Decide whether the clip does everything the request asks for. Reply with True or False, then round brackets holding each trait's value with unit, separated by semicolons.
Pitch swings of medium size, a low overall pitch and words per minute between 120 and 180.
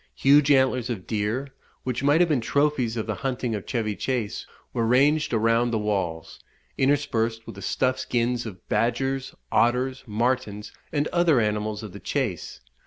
True (3.8 semitones; 120 Hz; 165 wpm)